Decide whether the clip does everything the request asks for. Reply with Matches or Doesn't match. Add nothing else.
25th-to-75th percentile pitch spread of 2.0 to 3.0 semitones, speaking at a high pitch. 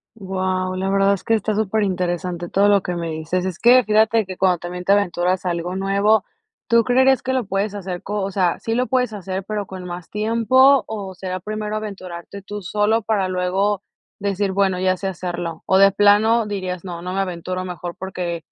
Matches